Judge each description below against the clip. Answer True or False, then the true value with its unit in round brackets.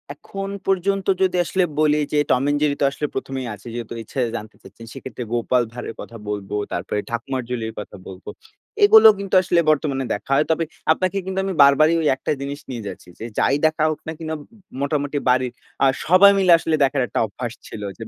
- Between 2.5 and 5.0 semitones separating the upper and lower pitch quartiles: False (5.6 semitones)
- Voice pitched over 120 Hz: True (140 Hz)